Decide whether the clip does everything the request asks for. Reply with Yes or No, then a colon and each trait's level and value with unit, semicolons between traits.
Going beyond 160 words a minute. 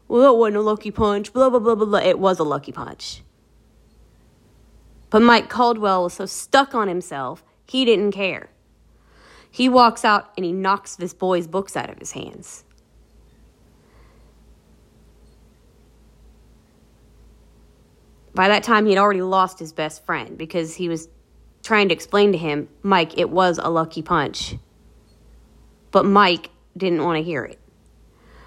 No: average, 150 wpm